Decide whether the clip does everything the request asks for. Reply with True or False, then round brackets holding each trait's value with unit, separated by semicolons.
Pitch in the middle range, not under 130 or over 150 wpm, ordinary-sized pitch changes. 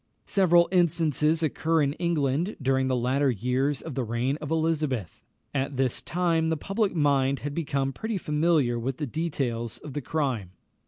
False (145 Hz; 165 wpm; 3.7 semitones)